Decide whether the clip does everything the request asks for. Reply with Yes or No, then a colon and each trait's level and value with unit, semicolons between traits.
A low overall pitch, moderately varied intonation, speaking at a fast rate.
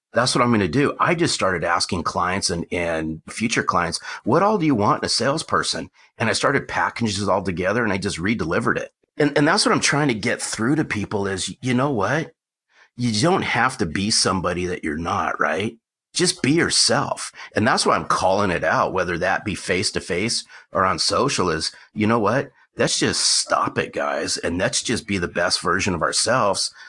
Yes: low, 100 Hz; average, 4.6 semitones; fast, 215 wpm